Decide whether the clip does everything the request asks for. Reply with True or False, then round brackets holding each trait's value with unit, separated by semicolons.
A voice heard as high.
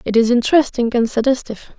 True (240 Hz)